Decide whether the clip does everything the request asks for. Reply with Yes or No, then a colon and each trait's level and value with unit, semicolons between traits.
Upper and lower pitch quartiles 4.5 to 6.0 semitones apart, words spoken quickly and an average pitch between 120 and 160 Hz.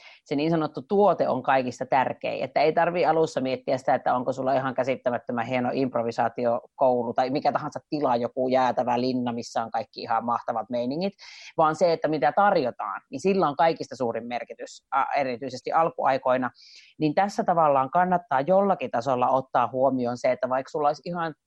Yes: average, 5.0 semitones; fast, 170 wpm; low, 135 Hz